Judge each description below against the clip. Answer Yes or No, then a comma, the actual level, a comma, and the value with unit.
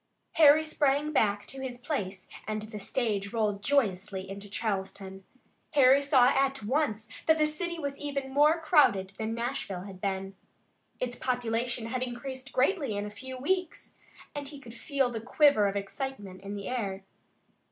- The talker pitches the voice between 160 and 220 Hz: No, high, 245 Hz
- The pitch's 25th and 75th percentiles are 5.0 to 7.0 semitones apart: Yes, wide, 5.6 semitones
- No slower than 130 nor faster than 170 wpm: Yes, average, 165 wpm